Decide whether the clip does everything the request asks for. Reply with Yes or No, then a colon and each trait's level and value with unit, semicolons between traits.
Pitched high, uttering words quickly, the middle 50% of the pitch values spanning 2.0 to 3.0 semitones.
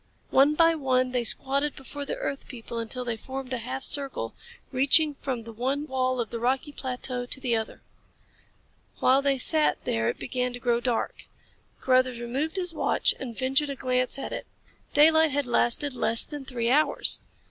No: very high, 260 Hz; average, 180 wpm; narrow, 2.5 semitones